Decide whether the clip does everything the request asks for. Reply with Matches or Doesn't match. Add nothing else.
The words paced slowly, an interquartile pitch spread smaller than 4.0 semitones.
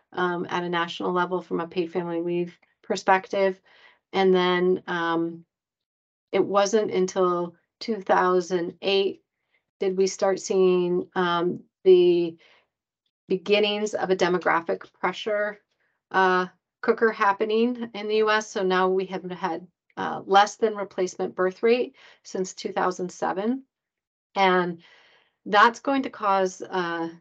Matches